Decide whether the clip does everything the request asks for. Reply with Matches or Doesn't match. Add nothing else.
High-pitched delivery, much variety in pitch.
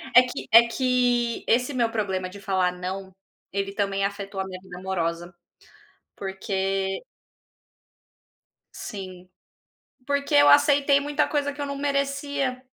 Matches